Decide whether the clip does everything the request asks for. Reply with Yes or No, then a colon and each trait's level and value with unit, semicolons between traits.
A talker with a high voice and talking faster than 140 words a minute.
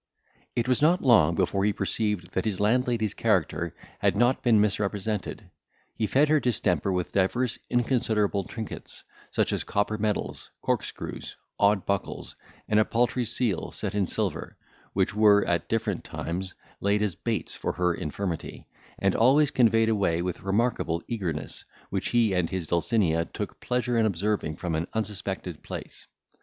No: low, 105 Hz; average, 155 wpm